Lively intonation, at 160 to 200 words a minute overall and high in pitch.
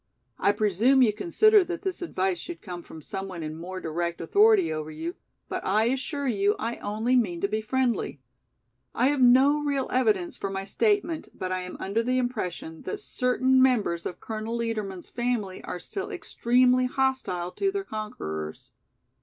Yes: wide, 5.8 semitones; average, 175 wpm; high, 220 Hz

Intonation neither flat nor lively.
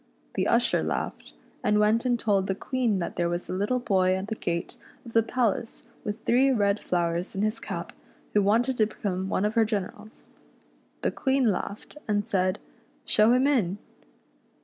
Yes: average, 3.5 semitones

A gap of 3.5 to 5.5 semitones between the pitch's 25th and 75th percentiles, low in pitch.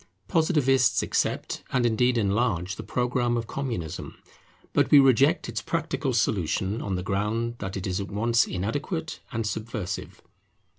Yes: average, 4.6 semitones; low, 115 Hz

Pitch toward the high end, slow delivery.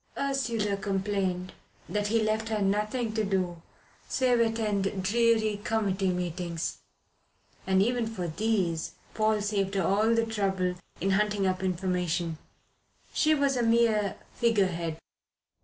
Yes: high, 205 Hz; slow, 125 wpm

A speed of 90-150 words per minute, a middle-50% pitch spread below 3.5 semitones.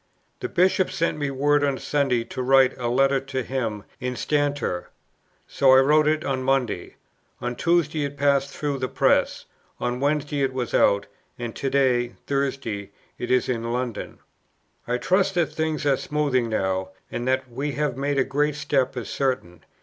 No: average, 175 wpm; average, 2.8 semitones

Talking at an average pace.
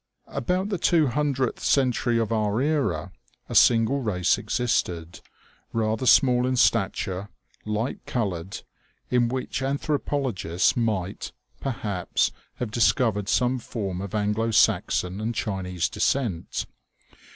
No: slow, 125 wpm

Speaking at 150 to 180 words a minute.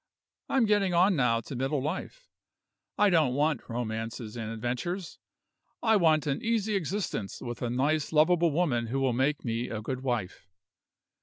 Yes: average, 160 wpm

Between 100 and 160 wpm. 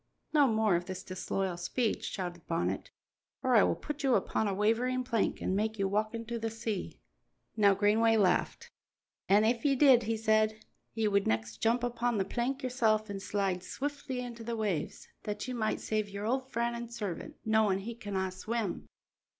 No: average, 185 wpm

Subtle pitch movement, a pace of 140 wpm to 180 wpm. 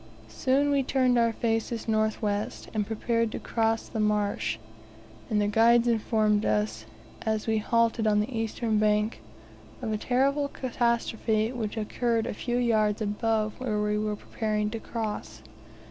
Yes: narrow, 1.8 semitones; average, 150 wpm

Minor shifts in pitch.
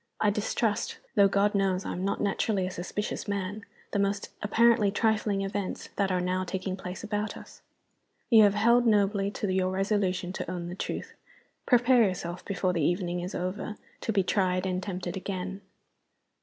Yes: narrow, 2.1 semitones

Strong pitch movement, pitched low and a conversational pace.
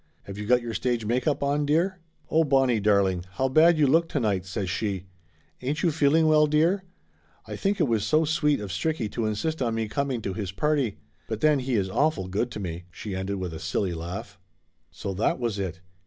No: wide, 7.3 semitones; low, 120 Hz; fast, 220 wpm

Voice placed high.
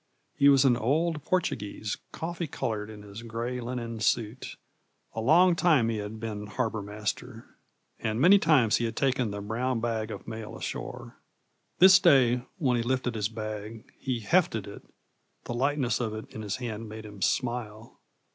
No: low, 115 Hz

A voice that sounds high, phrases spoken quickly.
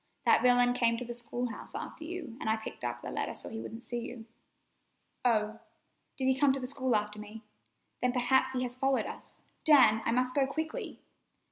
Yes: high, 245 Hz; fast, 210 wpm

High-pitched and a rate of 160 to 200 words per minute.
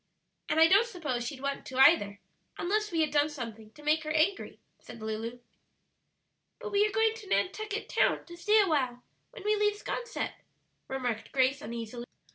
Yes: very high, 305 Hz; average, 180 wpm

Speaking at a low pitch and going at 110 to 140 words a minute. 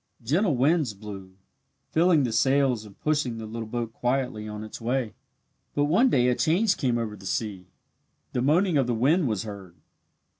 No: low, 125 Hz; average, 180 wpm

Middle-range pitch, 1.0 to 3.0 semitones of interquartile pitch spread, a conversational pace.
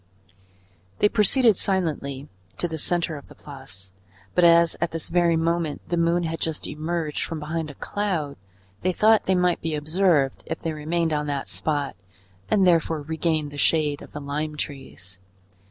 Yes: medium, 160 Hz; average, 2.7 semitones; average, 170 wpm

